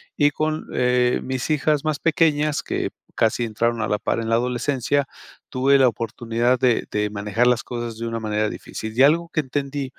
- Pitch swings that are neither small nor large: Yes, average, 3.8 semitones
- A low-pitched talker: Yes, low, 125 Hz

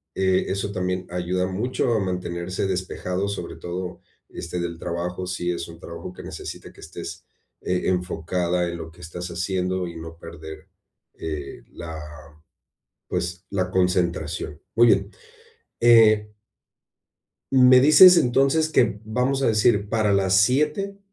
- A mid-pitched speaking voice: No, very low, 90 Hz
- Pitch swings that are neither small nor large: Yes, average, 3.7 semitones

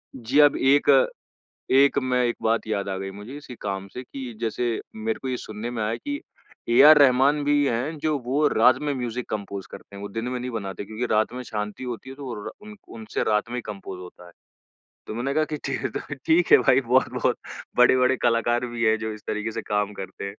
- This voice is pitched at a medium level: No, low, 120 Hz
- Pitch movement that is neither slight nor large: Yes, average, 3.6 semitones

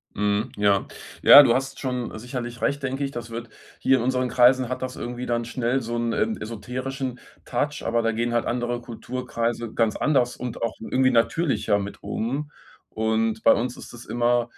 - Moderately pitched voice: No, low, 120 Hz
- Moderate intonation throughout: No, narrow, 1.8 semitones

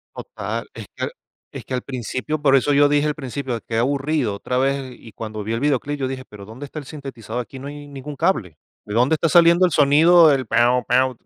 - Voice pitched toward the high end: No, low, 135 Hz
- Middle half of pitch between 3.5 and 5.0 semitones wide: No, average, 3.0 semitones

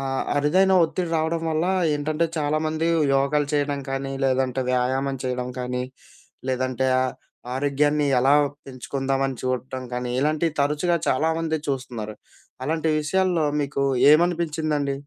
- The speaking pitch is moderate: Yes, medium, 145 Hz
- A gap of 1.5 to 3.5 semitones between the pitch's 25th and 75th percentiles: Yes, average, 3.1 semitones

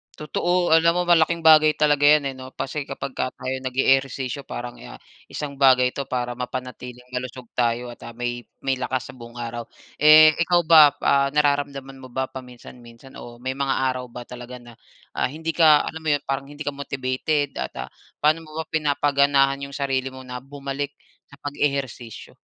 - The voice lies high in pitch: No, low, 135 Hz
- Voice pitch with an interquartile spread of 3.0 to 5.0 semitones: No, narrow, 2.6 semitones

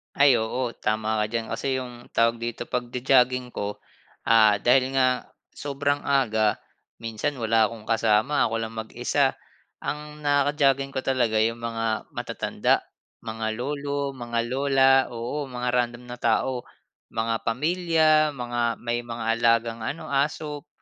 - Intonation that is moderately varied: Yes, average, 3.2 semitones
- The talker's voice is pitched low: Yes, low, 120 Hz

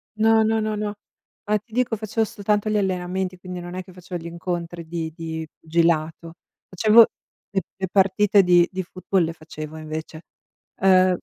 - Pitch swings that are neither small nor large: Yes, average, 3.6 semitones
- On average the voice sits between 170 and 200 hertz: Yes, medium, 185 Hz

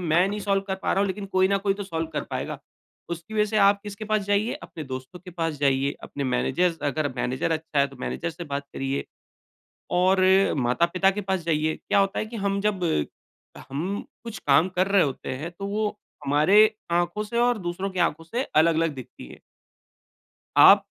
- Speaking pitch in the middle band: Yes, medium, 180 Hz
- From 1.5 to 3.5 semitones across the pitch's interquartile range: No, average, 4.4 semitones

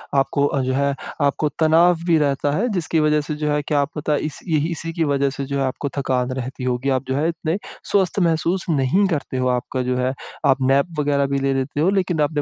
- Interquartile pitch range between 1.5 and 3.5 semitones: Yes, average, 2.9 semitones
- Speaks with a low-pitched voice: No, medium, 145 Hz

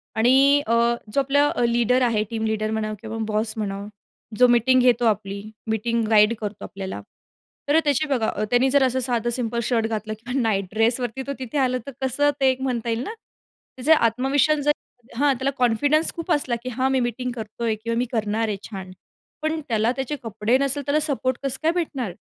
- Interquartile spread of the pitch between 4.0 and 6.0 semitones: No, average, 3.4 semitones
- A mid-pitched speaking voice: No, high, 245 Hz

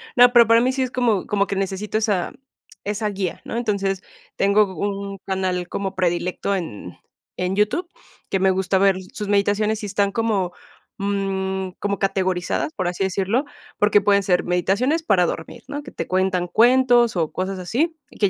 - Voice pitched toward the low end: No, high, 200 Hz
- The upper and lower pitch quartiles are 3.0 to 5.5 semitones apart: No, narrow, 2.4 semitones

